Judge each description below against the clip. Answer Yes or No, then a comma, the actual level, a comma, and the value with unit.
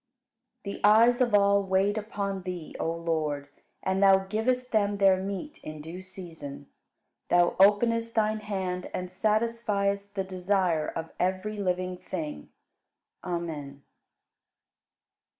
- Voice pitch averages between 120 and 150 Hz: No, high, 190 Hz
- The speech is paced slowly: Yes, slow, 125 wpm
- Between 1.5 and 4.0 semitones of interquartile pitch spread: Yes, average, 2.7 semitones